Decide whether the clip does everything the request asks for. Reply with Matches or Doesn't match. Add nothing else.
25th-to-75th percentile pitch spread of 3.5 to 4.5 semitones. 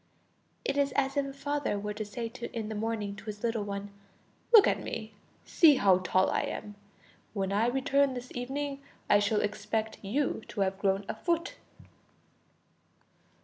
Doesn't match